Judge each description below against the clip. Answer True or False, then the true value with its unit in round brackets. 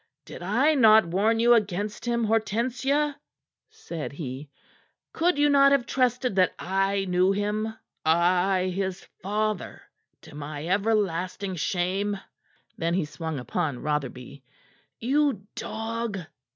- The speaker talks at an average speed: False (120 wpm)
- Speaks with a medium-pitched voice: False (200 Hz)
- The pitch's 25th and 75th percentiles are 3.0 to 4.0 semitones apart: False (4.6 semitones)